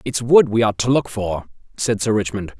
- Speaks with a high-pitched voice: No, low, 110 Hz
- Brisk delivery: Yes, fast, 230 wpm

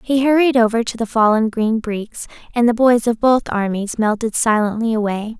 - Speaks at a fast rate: No, average, 190 wpm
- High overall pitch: Yes, high, 225 Hz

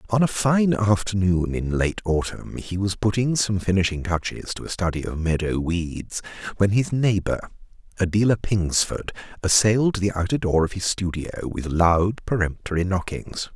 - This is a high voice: No, very low, 95 Hz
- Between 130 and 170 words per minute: Yes, average, 155 wpm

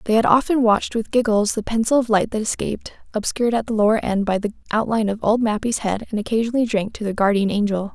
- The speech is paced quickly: Yes, fast, 235 wpm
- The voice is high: Yes, high, 220 Hz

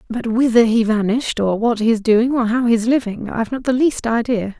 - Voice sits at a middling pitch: No, high, 230 Hz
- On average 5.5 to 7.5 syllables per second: Yes, 5.7 syllables/s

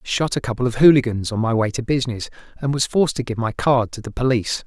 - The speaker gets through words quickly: Yes, fast, 255 wpm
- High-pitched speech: No, low, 120 Hz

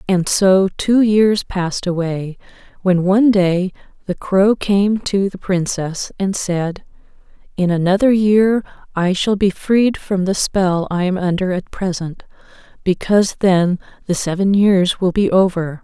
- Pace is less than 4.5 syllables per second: Yes, 4.0 syllables/s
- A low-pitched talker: No, high, 190 Hz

